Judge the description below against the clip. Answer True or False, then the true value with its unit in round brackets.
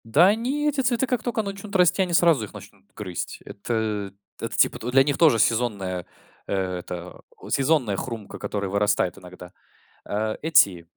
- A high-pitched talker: False (115 Hz)